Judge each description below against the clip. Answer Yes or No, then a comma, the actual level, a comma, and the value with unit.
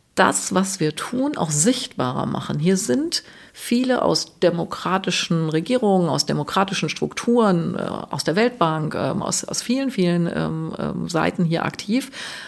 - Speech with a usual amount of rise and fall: No, wide, 6.5 semitones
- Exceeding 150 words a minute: No, slow, 125 wpm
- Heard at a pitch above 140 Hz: Yes, medium, 185 Hz